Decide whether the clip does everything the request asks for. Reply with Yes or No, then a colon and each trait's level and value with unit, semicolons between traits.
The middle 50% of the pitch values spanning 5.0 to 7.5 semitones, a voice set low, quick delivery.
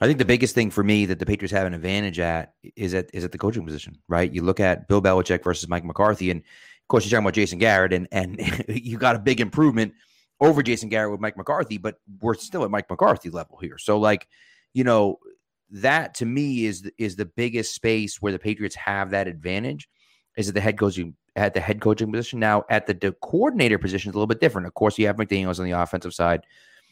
No: average, 3.1 semitones; low, 105 Hz; fast, 240 wpm